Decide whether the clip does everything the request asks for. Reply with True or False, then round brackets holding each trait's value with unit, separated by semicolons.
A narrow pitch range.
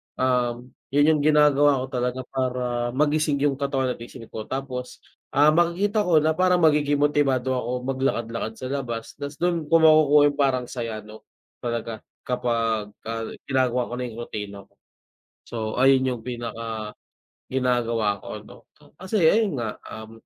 False (3.8 semitones)